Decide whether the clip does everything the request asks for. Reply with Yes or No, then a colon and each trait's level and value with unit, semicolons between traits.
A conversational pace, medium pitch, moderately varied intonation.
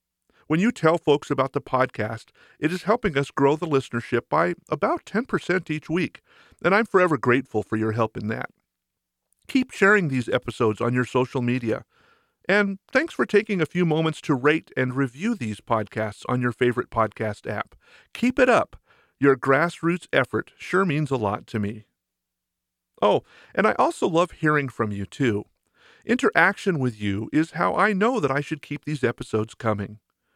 No: average, 175 wpm; medium, 145 Hz; wide, 7.1 semitones